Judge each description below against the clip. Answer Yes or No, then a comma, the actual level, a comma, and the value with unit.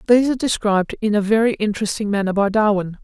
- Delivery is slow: No, average, 200 wpm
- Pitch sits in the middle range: No, high, 210 Hz